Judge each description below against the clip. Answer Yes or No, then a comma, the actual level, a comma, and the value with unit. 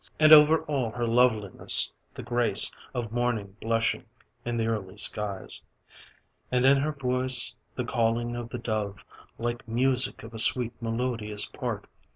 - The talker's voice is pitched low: Yes, low, 120 Hz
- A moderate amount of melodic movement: No, narrow, 2.1 semitones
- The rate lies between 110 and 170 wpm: Yes, average, 150 wpm